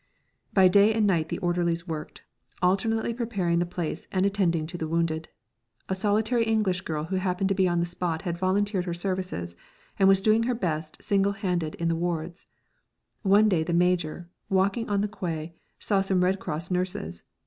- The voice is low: No, medium, 180 Hz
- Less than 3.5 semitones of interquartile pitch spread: Yes, average, 2.8 semitones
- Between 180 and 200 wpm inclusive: Yes, average, 185 wpm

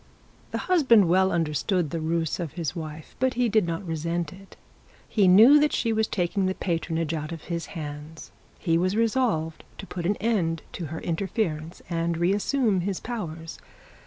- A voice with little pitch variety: No, average, 4.1 semitones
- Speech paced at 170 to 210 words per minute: Yes, average, 180 wpm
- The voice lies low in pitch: No, medium, 175 Hz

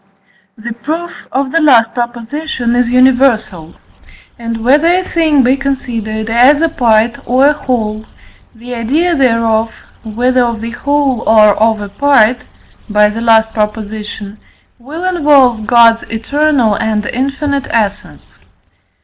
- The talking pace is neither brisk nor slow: No, slow, 130 wpm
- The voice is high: Yes, high, 240 Hz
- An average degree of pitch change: Yes, average, 3.9 semitones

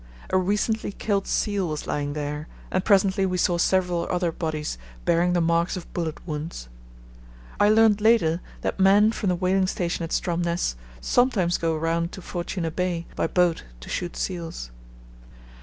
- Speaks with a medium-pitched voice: Yes, medium, 175 Hz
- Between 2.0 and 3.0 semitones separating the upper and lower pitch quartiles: Yes, narrow, 2.6 semitones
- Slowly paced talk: No, average, 160 wpm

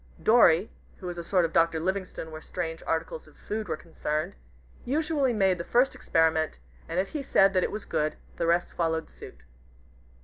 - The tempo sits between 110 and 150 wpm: No, average, 190 wpm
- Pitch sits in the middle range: Yes, medium, 170 Hz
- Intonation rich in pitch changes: No, average, 3.6 semitones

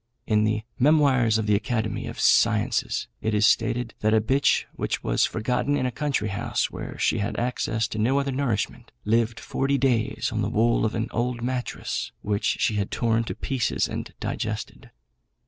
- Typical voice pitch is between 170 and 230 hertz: No, low, 115 Hz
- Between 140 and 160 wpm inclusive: No, average, 180 wpm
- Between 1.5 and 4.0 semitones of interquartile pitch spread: Yes, average, 2.8 semitones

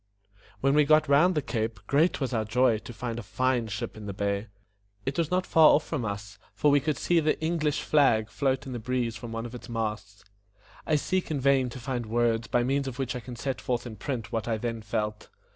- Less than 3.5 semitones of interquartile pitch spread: No, average, 4.0 semitones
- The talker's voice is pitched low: Yes, low, 120 Hz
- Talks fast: Yes, fast, 245 wpm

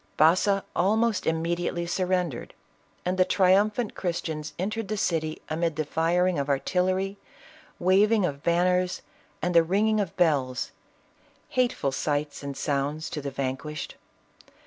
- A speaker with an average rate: No, slow, 130 wpm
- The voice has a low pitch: No, medium, 175 Hz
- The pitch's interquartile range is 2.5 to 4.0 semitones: Yes, average, 3.6 semitones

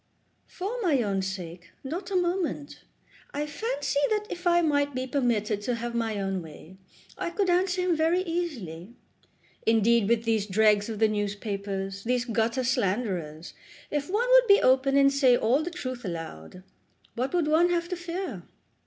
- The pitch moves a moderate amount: No, wide, 8.7 semitones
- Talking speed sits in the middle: Yes, average, 170 wpm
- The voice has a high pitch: Yes, very high, 250 Hz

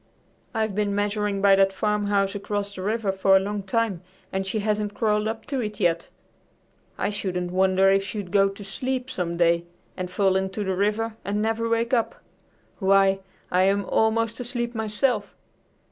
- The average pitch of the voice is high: Yes, high, 205 Hz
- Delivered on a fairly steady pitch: Yes, narrow, 2.3 semitones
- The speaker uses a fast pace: No, average, 175 wpm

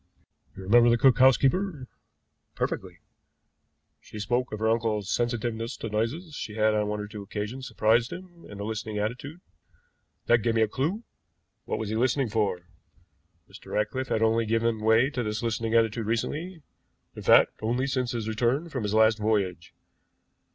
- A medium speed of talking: Yes, average, 170 wpm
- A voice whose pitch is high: No, low, 115 Hz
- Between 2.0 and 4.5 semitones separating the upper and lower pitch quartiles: Yes, average, 3.0 semitones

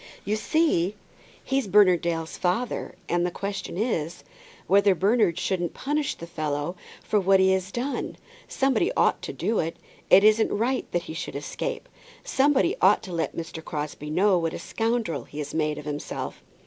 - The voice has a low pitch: No, high, 190 Hz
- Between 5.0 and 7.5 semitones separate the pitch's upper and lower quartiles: Yes, wide, 5.4 semitones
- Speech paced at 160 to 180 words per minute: Yes, average, 170 wpm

